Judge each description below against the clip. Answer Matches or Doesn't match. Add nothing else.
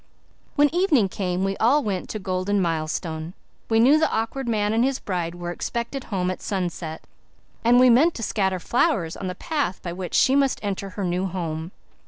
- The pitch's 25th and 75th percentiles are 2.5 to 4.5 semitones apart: Doesn't match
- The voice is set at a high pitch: Matches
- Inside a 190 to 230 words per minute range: Matches